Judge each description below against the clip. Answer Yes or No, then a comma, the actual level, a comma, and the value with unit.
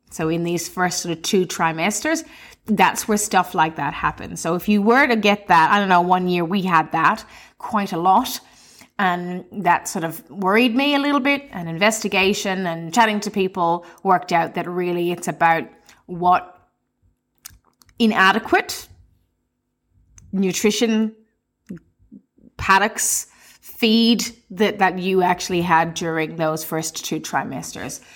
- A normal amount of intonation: Yes, average, 4.0 semitones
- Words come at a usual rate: Yes, average, 145 wpm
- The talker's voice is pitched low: No, medium, 185 Hz